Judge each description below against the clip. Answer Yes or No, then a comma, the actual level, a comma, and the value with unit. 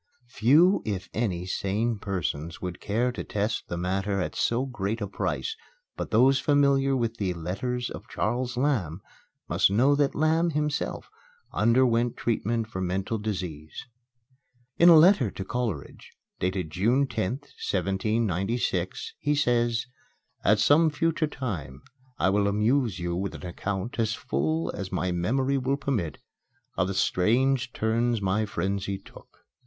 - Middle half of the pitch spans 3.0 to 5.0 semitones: No, wide, 5.4 semitones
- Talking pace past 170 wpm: No, average, 145 wpm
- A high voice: No, low, 110 Hz